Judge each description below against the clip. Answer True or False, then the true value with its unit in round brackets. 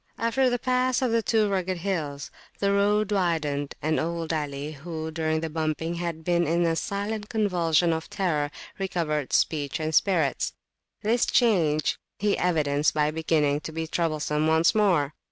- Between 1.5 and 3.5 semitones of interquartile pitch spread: False (4.4 semitones)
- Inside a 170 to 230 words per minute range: False (160 wpm)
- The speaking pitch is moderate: True (165 Hz)